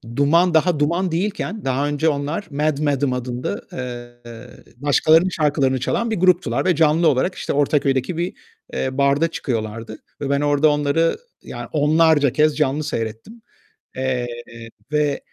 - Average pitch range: Yes, average, 3.7 semitones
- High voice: No, medium, 145 Hz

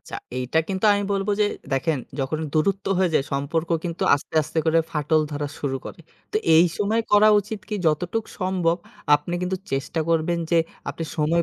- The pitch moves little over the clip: No, average, 4.0 semitones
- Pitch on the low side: No, medium, 165 Hz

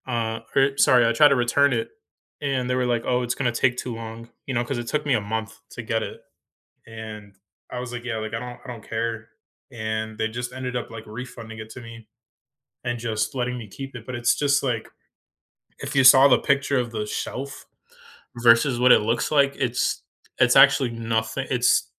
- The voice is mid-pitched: No, low, 120 Hz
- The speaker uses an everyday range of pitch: No, narrow, 2.2 semitones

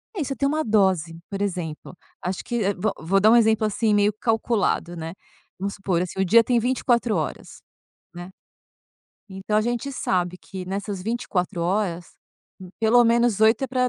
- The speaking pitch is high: Yes, high, 205 Hz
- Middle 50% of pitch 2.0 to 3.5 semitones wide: No, average, 4.2 semitones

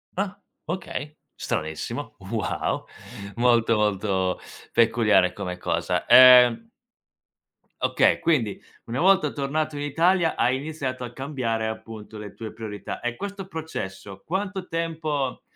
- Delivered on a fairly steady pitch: No, wide, 6.5 semitones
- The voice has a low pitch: Yes, low, 130 Hz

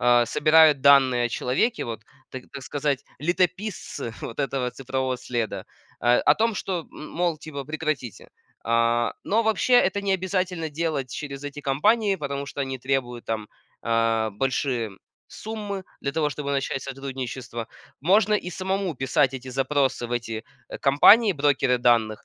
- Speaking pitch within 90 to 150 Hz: Yes, medium, 140 Hz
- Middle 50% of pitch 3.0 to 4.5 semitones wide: No, average, 5.3 semitones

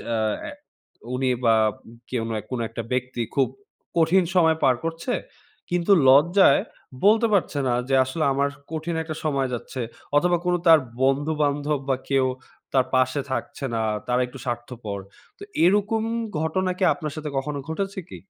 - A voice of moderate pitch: Yes, medium, 145 Hz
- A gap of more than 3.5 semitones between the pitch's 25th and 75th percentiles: Yes, average, 4.8 semitones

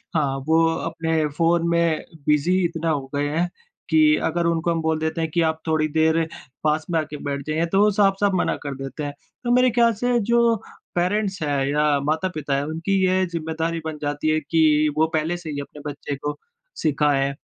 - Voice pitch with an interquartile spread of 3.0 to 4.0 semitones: No, narrow, 2.6 semitones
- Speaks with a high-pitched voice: No, medium, 160 Hz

